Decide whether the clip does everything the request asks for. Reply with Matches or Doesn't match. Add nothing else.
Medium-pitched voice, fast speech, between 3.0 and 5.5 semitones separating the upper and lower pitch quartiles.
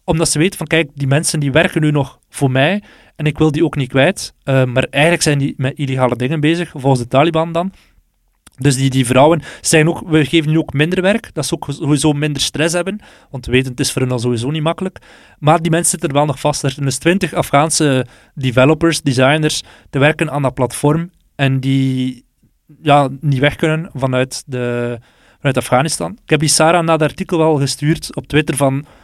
Matches